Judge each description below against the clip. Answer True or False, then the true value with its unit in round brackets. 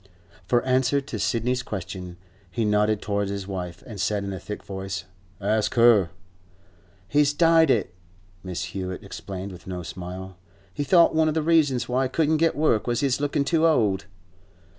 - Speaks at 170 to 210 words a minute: True (175 wpm)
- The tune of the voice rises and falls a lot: True (6.8 semitones)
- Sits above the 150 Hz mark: False (110 Hz)